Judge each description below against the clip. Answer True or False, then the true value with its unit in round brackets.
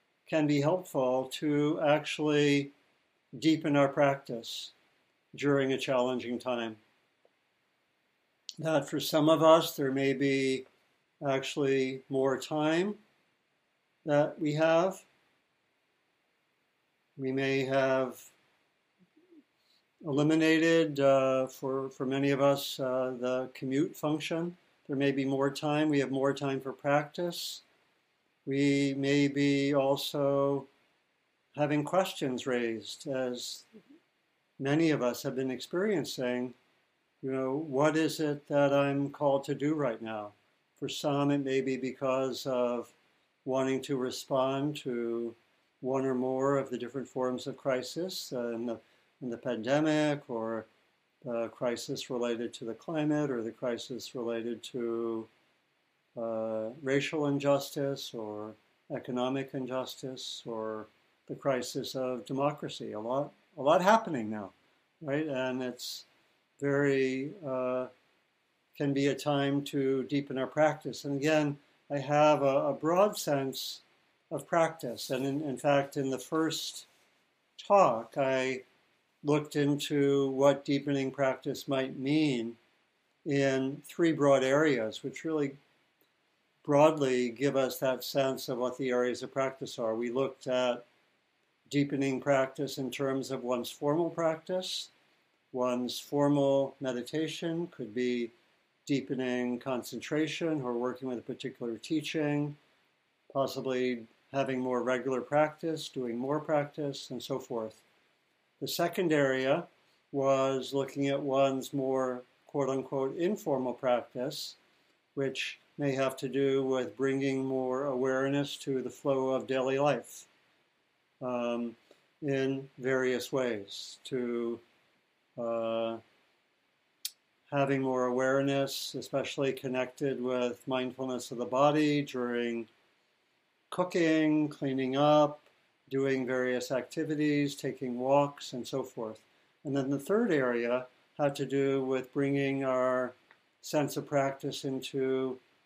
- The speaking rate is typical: False (120 wpm)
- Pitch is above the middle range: False (135 Hz)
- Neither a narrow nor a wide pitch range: False (2.2 semitones)